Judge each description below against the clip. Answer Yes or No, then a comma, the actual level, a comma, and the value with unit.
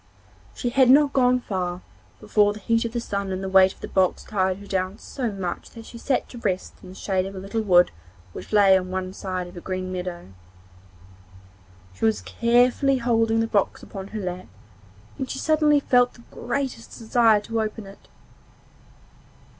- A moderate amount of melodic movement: Yes, average, 4.2 semitones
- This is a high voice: Yes, high, 210 Hz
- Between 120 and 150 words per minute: No, average, 190 wpm